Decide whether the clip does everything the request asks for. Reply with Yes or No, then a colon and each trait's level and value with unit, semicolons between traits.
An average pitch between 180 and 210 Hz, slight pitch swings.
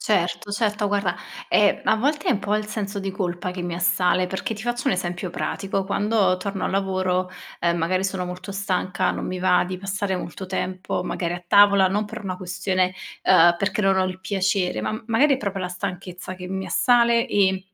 Yes: high, 190 Hz; narrow, 2.0 semitones